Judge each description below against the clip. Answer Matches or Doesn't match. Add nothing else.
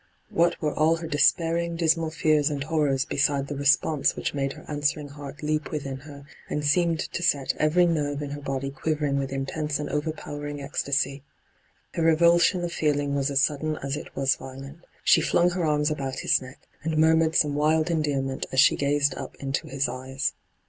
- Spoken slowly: Doesn't match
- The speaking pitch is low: Doesn't match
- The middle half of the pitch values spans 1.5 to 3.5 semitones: Matches